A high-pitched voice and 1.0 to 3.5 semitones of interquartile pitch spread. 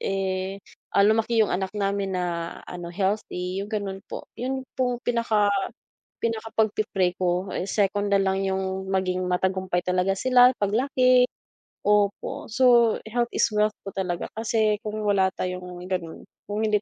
Yes: high, 200 Hz; average, 2.7 semitones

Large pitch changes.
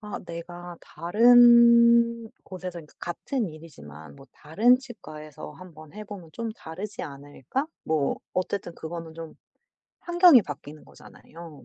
Yes: wide, 6.9 semitones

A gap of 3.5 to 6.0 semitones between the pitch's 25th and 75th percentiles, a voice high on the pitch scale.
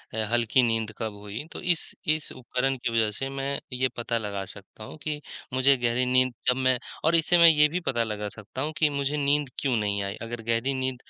No: average, 3.8 semitones; low, 125 Hz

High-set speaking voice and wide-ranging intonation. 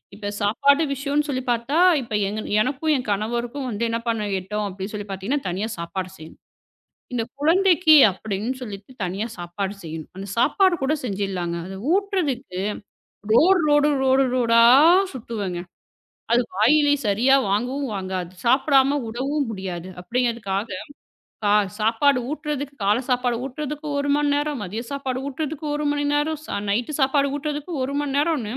Yes: high, 245 Hz; wide, 6.1 semitones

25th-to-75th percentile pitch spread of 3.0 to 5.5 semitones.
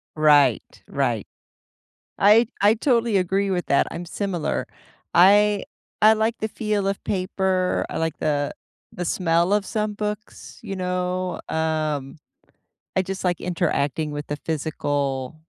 Yes: average, 4.7 semitones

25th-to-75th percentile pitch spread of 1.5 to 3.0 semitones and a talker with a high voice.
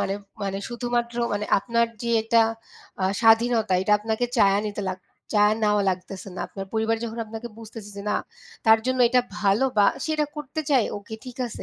Yes: narrow, 2.6 semitones; high, 220 Hz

